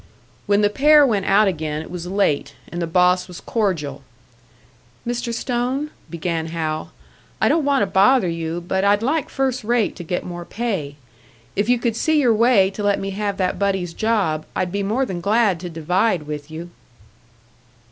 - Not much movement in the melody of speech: No, average, 5.2 semitones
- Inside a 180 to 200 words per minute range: Yes, average, 185 wpm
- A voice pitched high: Yes, high, 195 Hz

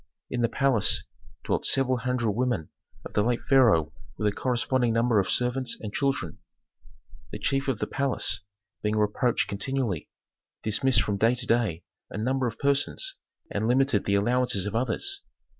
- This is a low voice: Yes, low, 120 Hz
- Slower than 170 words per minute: Yes, average, 160 wpm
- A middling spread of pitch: Yes, average, 3.7 semitones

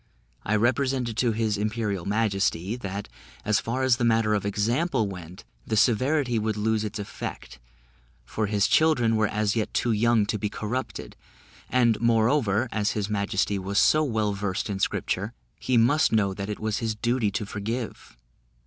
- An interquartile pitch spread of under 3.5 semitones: Yes, narrow, 2.5 semitones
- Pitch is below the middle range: Yes, low, 110 Hz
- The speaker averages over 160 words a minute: Yes, average, 170 wpm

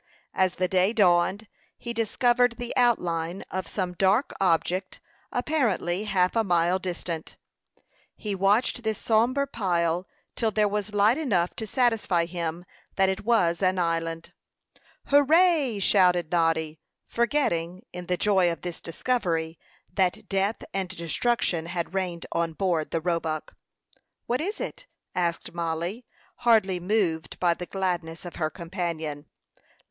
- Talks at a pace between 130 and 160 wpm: Yes, slow, 135 wpm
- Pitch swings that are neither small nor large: Yes, average, 4.5 semitones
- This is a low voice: No, medium, 185 Hz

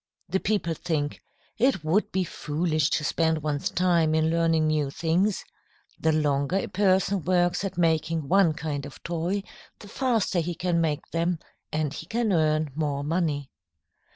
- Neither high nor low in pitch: Yes, medium, 165 Hz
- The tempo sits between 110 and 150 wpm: No, average, 160 wpm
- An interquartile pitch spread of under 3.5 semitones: Yes, average, 2.9 semitones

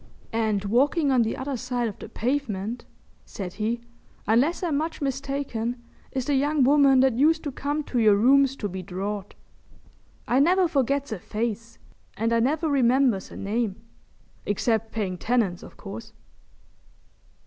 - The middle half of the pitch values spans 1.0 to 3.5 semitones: No, average, 4.3 semitones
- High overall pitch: Yes, high, 245 Hz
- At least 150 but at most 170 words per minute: Yes, average, 155 wpm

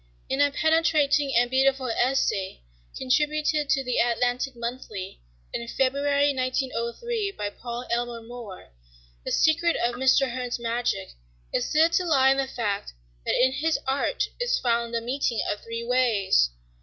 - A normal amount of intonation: Yes, average, 3.3 semitones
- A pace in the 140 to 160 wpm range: Yes, average, 150 wpm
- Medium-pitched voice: No, very high, 255 Hz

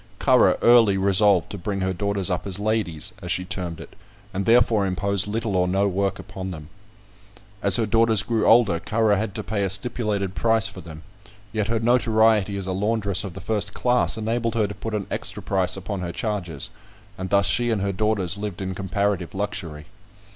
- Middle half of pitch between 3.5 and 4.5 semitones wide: No, average, 2.7 semitones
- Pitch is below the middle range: Yes, low, 100 Hz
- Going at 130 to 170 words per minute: No, average, 200 wpm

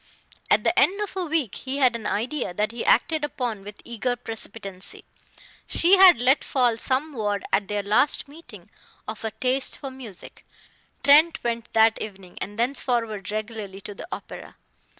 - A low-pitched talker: No, high, 235 Hz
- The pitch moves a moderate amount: Yes, average, 4.7 semitones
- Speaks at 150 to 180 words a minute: Yes, average, 170 wpm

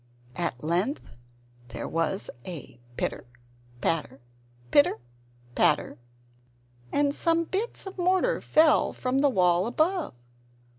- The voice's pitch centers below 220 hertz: No, very high, 255 Hz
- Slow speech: Yes, slow, 105 wpm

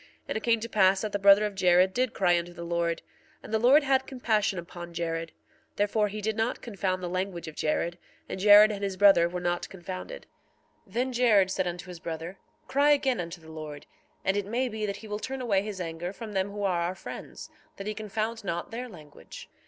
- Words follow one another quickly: Yes, fast, 230 wpm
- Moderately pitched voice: No, high, 195 Hz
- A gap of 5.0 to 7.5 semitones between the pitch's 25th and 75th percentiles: No, average, 3.8 semitones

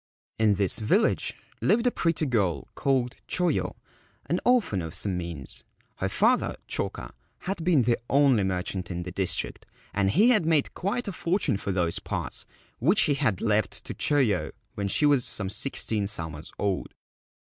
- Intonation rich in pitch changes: Yes, wide, 8.7 semitones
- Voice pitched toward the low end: Yes, low, 110 Hz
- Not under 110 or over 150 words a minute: No, average, 165 wpm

